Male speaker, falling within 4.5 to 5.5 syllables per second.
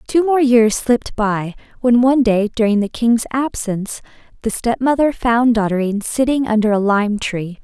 No: female; 5.0 syllables/s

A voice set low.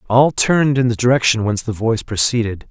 Yes: low, 115 Hz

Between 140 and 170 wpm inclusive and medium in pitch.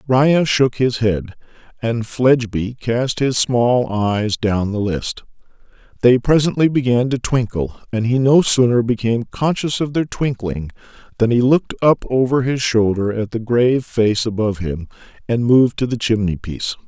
No: average, 165 wpm; low, 120 Hz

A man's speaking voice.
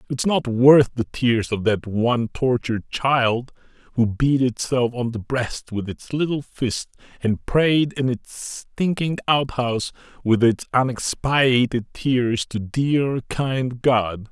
Yes: male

